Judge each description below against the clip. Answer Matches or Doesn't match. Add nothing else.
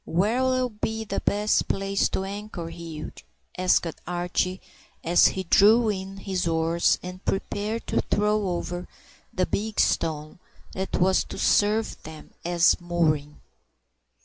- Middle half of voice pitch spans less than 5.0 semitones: Matches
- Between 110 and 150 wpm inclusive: Matches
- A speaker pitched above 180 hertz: Matches